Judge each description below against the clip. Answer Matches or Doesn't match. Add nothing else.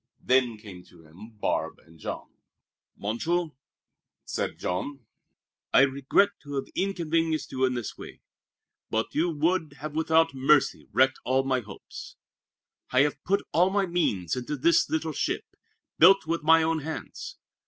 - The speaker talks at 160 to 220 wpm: Doesn't match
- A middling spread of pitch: Matches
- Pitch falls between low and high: Matches